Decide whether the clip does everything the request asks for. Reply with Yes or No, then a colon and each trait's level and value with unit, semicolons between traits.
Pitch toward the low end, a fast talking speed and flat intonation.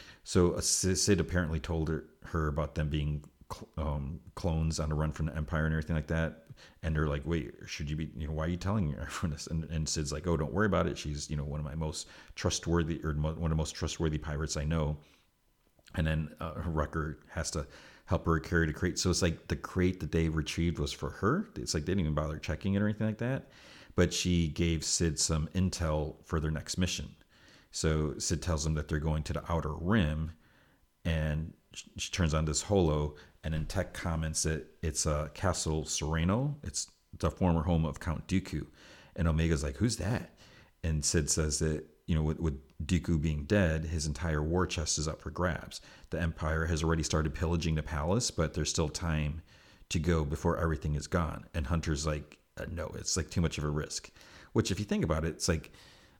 Yes: very low, 80 Hz; fast, 215 wpm; narrow, 1.9 semitones